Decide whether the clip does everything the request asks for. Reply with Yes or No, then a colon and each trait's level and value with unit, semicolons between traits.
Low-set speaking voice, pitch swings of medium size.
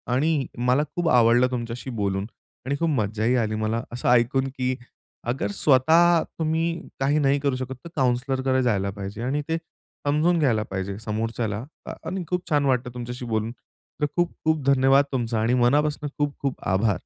Yes: low, 130 Hz; average, 4.2 semitones